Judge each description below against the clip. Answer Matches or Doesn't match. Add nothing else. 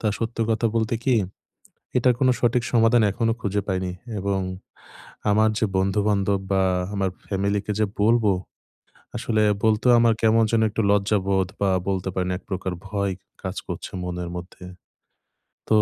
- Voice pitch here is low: Matches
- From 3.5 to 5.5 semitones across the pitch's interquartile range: Doesn't match